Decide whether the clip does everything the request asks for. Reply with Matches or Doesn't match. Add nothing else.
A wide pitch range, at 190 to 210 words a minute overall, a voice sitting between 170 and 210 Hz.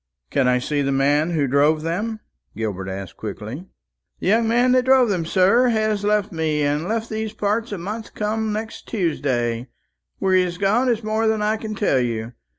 Matches